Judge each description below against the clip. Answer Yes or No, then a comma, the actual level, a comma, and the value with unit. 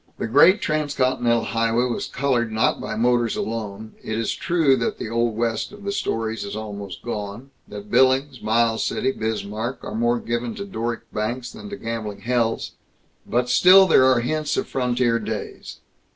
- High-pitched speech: No, low, 120 Hz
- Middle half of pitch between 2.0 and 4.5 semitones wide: Yes, average, 2.8 semitones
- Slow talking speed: No, average, 170 wpm